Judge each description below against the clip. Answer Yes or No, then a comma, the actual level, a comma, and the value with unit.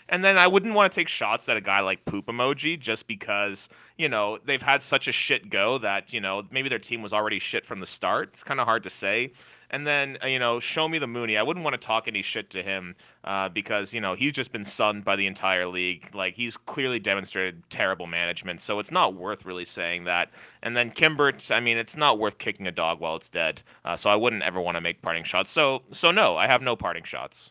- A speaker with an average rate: No, fast, 255 wpm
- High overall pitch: No, low, 110 Hz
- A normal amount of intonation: No, wide, 5.7 semitones